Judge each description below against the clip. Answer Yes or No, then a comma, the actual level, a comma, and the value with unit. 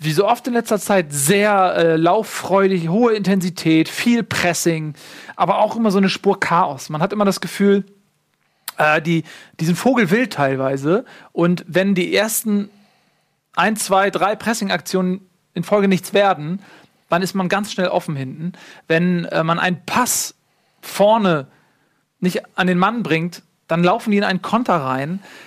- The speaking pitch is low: No, high, 190 Hz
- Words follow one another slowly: No, average, 160 wpm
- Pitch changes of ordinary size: Yes, average, 3.2 semitones